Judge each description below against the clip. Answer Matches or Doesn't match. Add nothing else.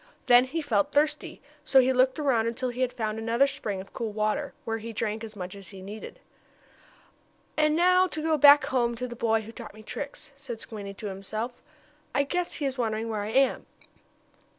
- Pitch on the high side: Matches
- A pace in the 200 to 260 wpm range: Matches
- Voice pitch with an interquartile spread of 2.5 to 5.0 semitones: Matches